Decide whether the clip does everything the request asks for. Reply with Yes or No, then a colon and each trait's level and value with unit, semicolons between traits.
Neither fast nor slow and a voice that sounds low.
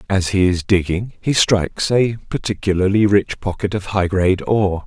Yes: average, 175 wpm; low, 100 Hz